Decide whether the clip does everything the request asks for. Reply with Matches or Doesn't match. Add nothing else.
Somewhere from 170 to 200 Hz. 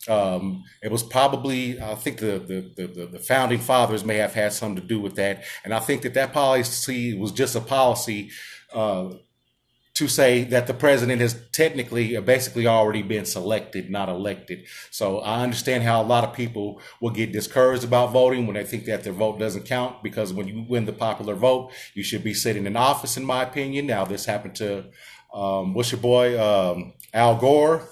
Doesn't match